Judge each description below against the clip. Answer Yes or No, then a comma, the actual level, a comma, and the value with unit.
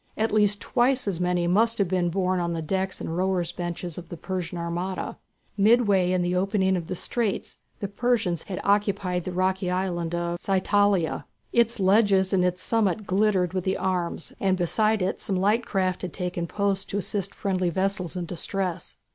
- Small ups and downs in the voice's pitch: Yes, narrow, 2.2 semitones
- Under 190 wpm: Yes, average, 180 wpm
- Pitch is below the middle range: No, medium, 185 Hz